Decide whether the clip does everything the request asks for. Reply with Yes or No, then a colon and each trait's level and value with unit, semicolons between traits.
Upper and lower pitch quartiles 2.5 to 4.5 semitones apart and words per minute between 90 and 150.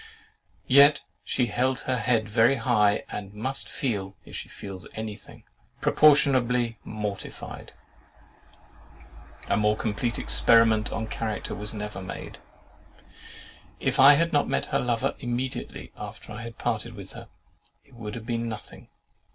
Yes: average, 3.1 semitones; slow, 135 wpm